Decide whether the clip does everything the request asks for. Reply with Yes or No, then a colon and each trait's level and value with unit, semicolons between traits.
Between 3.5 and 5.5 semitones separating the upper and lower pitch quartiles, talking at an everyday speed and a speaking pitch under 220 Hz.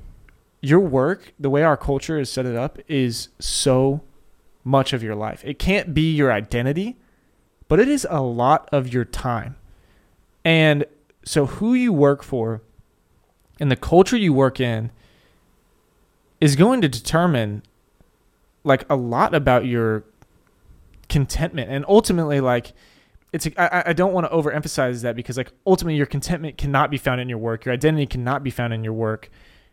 Yes: average, 4.7 semitones; average, 165 wpm; low, 135 Hz